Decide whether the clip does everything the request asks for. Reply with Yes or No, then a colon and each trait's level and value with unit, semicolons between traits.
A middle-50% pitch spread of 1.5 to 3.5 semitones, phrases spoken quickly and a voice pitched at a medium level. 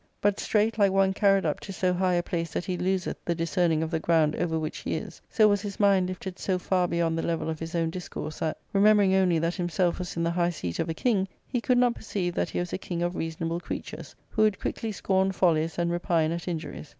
Yes: average, 2.7 semitones; fast, 250 wpm; medium, 175 Hz